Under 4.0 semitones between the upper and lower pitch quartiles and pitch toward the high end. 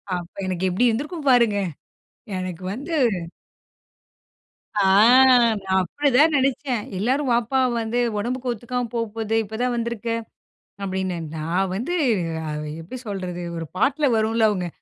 No: average, 4.8 semitones; high, 230 Hz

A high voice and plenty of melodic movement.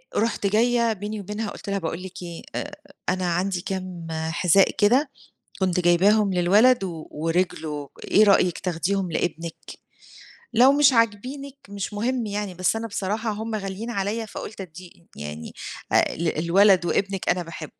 No: high, 195 Hz; average, 3.7 semitones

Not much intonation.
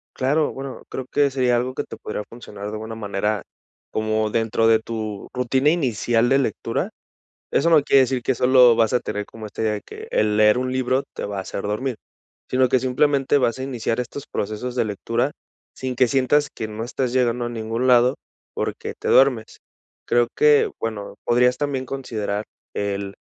No: average, 3.2 semitones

